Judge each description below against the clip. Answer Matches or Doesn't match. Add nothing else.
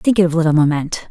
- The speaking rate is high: Matches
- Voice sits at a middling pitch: Matches